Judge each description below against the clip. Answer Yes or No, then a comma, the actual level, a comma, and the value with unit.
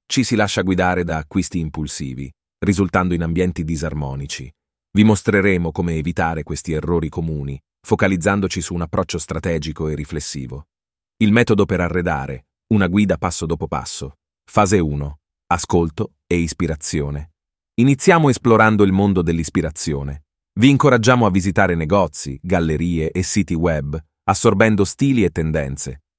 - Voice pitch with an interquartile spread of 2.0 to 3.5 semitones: No, average, 4.4 semitones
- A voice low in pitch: Yes, very low, 85 Hz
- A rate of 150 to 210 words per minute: No, average, 130 wpm